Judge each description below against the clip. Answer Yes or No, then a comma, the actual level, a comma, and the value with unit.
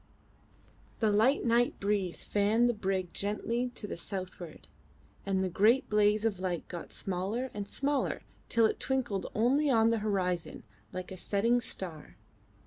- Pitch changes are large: No, average, 3.7 semitones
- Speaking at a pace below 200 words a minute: Yes, average, 150 wpm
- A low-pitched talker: No, high, 210 Hz